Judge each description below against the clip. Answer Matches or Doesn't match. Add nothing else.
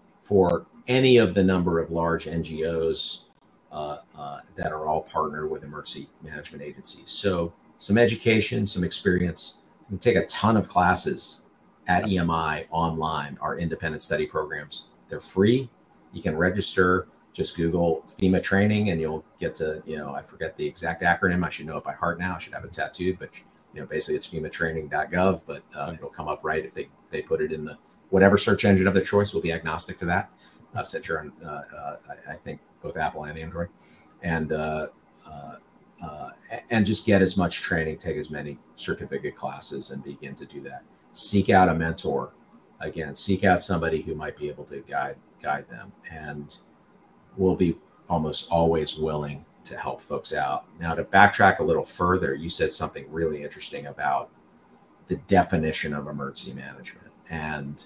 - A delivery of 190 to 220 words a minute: Doesn't match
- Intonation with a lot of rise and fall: Doesn't match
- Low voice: Matches